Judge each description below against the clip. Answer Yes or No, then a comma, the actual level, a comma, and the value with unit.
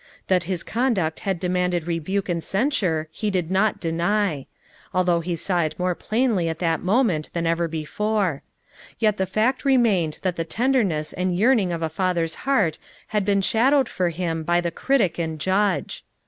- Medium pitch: Yes, medium, 180 Hz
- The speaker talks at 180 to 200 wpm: Yes, average, 185 wpm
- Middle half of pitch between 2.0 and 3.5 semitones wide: No, average, 4.1 semitones